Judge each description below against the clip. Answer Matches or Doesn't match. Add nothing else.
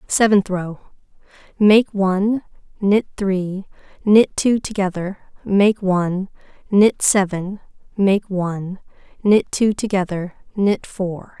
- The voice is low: Doesn't match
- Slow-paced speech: Matches